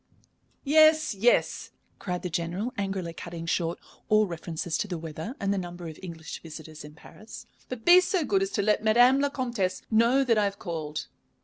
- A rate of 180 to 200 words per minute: Yes, average, 190 wpm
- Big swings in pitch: Yes, wide, 6.4 semitones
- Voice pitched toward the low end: No, high, 195 Hz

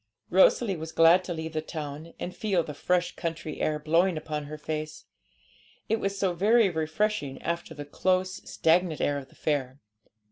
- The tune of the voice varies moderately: Yes, average, 3.2 semitones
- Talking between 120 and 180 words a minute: Yes, average, 175 wpm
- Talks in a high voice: No, medium, 160 Hz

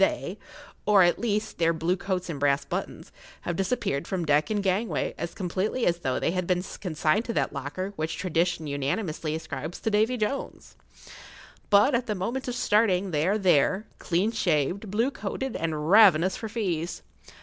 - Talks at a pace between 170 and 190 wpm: Yes, average, 180 wpm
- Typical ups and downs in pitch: Yes, average, 4.6 semitones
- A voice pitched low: No, medium, 185 Hz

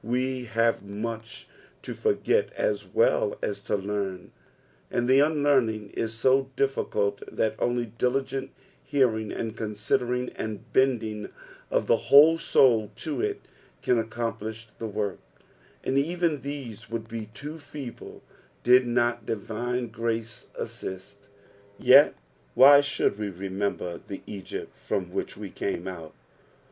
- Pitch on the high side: No, low, 115 Hz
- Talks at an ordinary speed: No, slow, 130 wpm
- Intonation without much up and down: No, average, 4.1 semitones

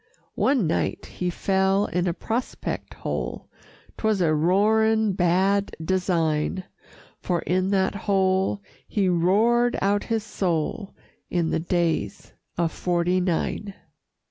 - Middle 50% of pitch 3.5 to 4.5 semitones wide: No, average, 2.7 semitones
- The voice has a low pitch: No, high, 190 Hz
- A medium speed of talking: No, slow, 115 wpm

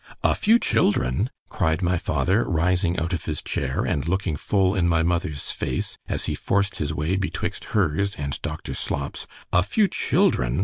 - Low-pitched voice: Yes, very low, 85 Hz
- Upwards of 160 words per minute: Yes, average, 170 wpm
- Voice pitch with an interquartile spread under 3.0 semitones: No, average, 4.2 semitones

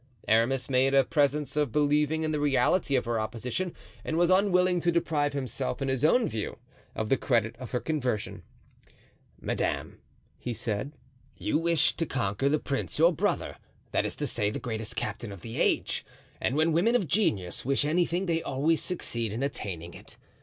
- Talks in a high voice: No, medium, 140 Hz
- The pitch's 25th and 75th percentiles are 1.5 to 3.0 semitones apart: No, wide, 5.6 semitones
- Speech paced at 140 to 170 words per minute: No, average, 180 wpm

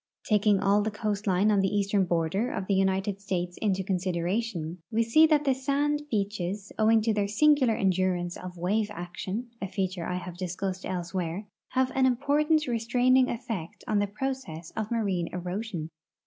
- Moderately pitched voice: No, high, 200 Hz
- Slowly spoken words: No, average, 165 wpm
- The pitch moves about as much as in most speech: Yes, average, 4.1 semitones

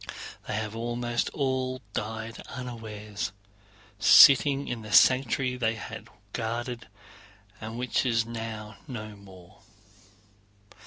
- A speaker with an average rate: No, slow, 105 wpm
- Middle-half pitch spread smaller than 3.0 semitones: Yes, narrow, 2.6 semitones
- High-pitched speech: No, low, 115 Hz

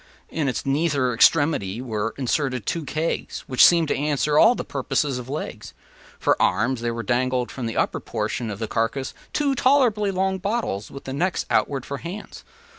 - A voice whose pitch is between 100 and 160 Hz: Yes, low, 135 Hz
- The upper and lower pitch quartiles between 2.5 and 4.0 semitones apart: No, wide, 5.6 semitones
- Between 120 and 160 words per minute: No, average, 180 wpm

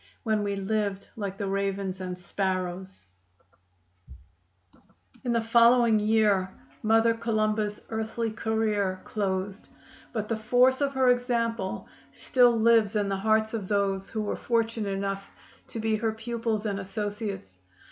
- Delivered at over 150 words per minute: No, slow, 135 wpm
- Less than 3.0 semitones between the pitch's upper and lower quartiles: Yes, narrow, 2.4 semitones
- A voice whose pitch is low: No, high, 215 Hz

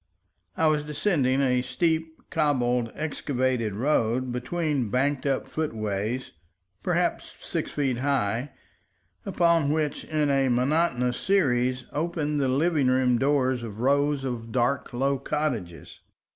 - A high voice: No, low, 135 Hz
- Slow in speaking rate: Yes, slow, 120 wpm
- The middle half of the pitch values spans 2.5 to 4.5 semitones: Yes, average, 3.3 semitones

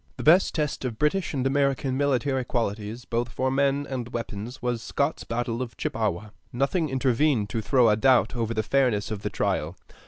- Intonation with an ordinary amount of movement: Yes, average, 3.3 semitones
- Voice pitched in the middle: No, low, 125 Hz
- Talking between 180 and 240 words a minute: Yes, average, 185 wpm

